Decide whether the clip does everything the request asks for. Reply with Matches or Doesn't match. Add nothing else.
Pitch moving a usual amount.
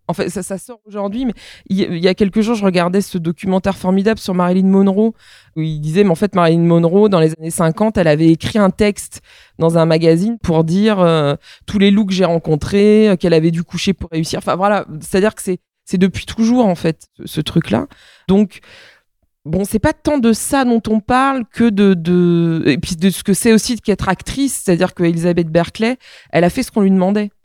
Matches